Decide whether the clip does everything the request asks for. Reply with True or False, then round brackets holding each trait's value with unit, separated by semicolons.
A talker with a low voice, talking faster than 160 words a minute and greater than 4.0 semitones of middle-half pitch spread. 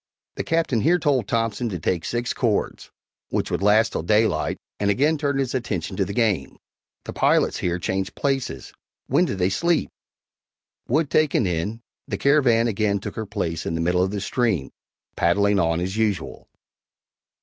True (105 Hz; 170 wpm; 5.0 semitones)